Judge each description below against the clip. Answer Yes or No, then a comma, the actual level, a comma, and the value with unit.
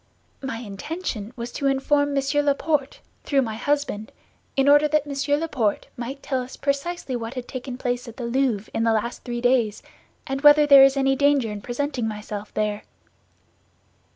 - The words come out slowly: No, average, 175 wpm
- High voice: Yes, very high, 265 Hz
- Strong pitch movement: No, average, 3.4 semitones